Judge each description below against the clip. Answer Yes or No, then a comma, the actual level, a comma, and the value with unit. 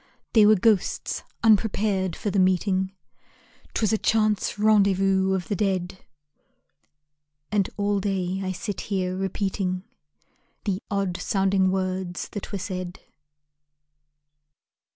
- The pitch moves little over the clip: Yes, narrow, 1.7 semitones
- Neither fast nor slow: No, slow, 110 wpm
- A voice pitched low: No, high, 195 Hz